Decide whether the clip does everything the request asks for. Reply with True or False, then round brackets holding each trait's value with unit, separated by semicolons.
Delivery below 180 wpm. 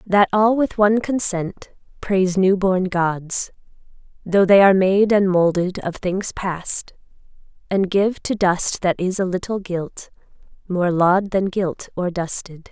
True (155 wpm)